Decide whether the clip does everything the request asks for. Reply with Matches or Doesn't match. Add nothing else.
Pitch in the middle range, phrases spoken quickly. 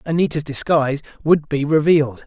Doesn't match